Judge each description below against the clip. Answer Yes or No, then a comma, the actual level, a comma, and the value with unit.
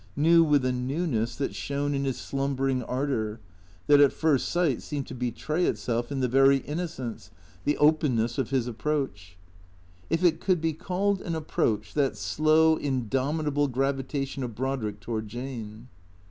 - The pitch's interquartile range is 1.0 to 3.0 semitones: No, average, 3.7 semitones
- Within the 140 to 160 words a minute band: Yes, average, 155 wpm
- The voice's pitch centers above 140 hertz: No, low, 135 Hz